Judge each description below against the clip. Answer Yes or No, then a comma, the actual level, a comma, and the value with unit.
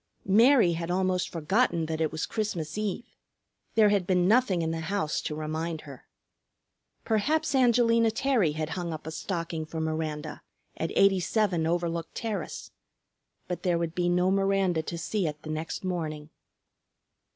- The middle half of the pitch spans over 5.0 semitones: No, average, 4.1 semitones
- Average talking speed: Yes, average, 155 wpm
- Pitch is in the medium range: Yes, medium, 175 Hz